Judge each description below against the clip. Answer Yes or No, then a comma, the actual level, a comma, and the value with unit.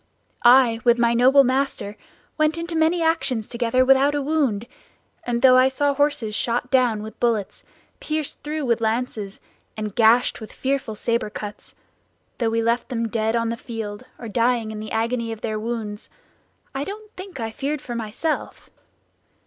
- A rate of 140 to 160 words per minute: No, average, 170 wpm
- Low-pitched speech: No, high, 240 Hz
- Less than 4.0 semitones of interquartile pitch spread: Yes, average, 3.5 semitones